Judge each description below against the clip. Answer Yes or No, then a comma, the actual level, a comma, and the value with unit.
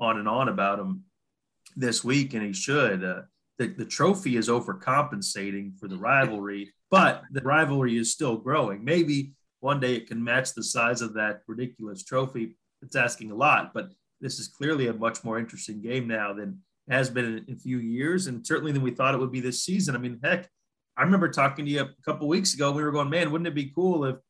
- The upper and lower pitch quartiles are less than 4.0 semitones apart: No, average, 4.5 semitones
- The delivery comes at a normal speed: No, fast, 220 wpm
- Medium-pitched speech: No, low, 130 Hz